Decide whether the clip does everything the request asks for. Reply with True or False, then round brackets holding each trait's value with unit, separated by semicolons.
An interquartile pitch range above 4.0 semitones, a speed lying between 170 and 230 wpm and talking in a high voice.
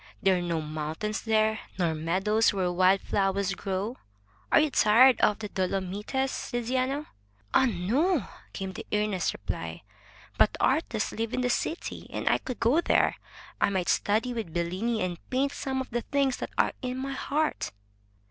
True (5.3 semitones; 175 wpm; 215 Hz)